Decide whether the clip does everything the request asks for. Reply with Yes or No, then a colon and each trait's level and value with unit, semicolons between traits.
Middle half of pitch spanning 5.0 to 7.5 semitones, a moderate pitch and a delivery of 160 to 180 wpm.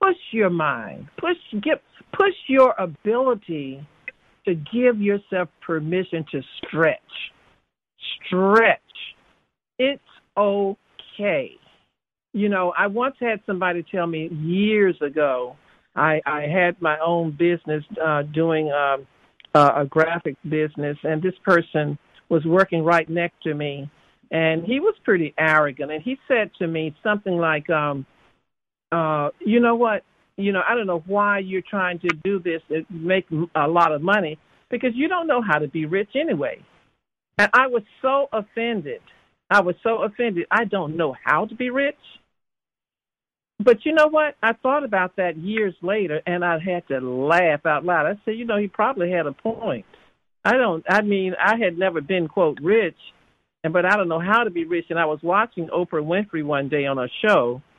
Yes: average, 5.3 semitones; medium, 180 Hz; average, 170 wpm